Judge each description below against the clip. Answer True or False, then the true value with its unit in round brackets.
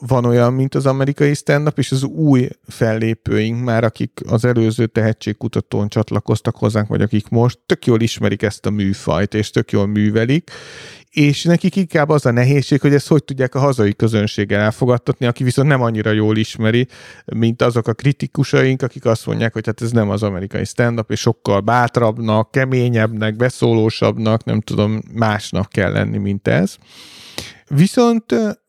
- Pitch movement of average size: True (3.6 semitones)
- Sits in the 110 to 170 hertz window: True (115 Hz)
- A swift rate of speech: True (160 wpm)